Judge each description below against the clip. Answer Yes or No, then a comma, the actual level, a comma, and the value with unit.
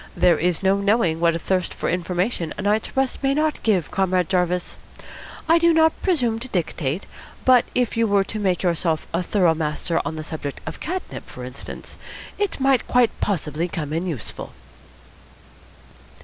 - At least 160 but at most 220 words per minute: Yes, average, 170 wpm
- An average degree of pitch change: No, wide, 6.3 semitones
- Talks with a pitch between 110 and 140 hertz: No, medium, 185 Hz